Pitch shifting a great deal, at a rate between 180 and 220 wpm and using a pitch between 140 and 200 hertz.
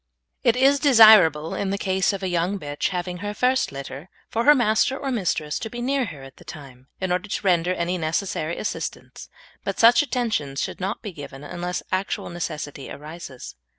Yes: wide, 6.1 semitones; average, 190 wpm; medium, 185 Hz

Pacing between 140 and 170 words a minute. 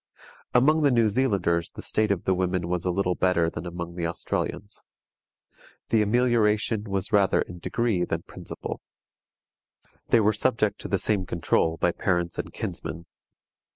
Yes: average, 155 wpm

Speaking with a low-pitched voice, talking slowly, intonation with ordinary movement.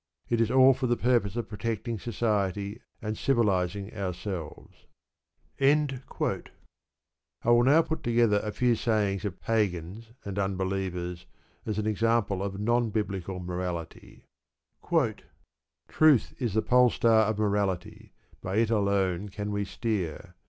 Yes: low, 105 Hz; slow, 130 wpm; average, 3.3 semitones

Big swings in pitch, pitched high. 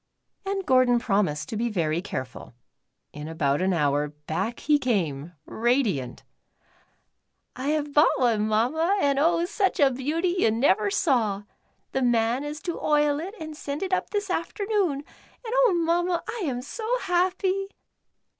Yes: wide, 8.7 semitones; very high, 275 Hz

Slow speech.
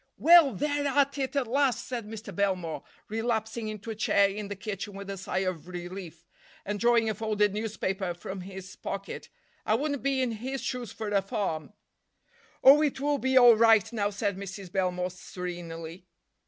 No: average, 180 wpm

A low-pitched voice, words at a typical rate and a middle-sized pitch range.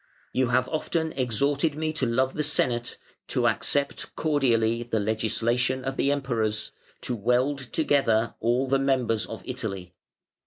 Yes: low, 125 Hz; average, 145 wpm; average, 3.4 semitones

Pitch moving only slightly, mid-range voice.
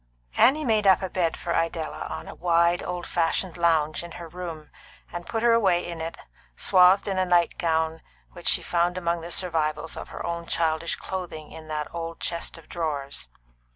Yes: narrow, 1.8 semitones; medium, 170 Hz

